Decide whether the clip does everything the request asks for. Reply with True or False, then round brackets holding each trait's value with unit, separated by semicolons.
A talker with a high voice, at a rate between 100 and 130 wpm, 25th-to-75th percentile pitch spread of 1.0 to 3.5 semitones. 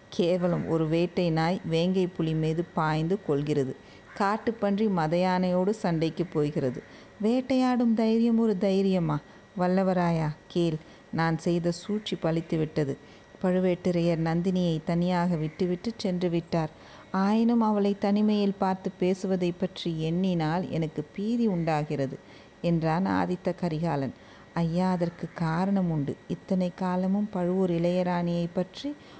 False (180 Hz; 110 wpm; 2.7 semitones)